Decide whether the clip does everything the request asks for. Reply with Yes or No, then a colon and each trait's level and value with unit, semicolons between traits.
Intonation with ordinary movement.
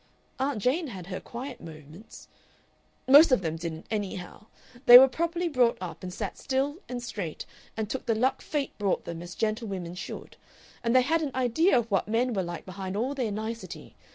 No: wide, 5.8 semitones